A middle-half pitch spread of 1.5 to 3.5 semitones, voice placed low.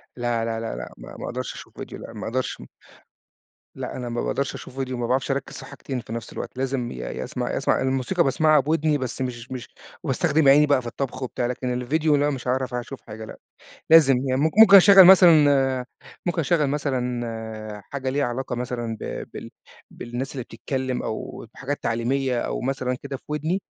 Yes: average, 2.9 semitones; low, 130 Hz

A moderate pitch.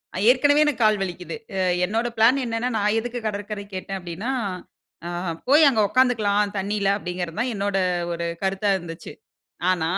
No: high, 205 Hz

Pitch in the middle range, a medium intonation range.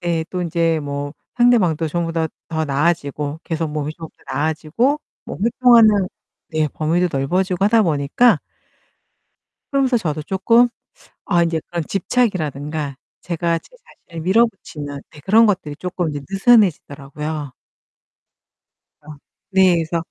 Yes: medium, 165 Hz; average, 4.2 semitones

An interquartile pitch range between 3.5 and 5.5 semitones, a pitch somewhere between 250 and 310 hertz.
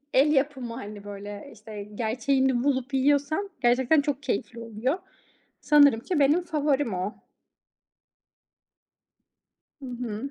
Yes: average, 4.3 semitones; very high, 260 Hz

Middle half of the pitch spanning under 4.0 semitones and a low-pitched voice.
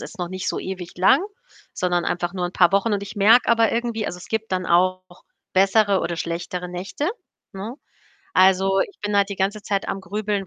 No: narrow, 2.5 semitones; high, 195 Hz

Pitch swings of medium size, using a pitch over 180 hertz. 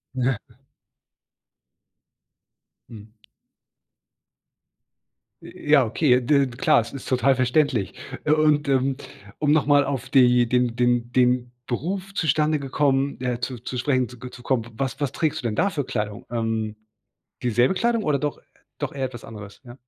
No: average, 3.1 semitones; low, 130 Hz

